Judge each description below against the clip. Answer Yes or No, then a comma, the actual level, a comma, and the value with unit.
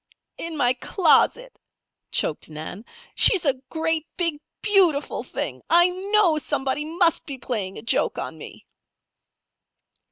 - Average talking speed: No, slow, 125 wpm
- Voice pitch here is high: Yes, very high, 320 Hz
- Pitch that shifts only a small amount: No, average, 5.2 semitones